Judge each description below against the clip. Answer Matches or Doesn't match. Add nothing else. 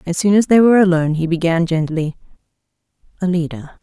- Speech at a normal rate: Matches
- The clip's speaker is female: Matches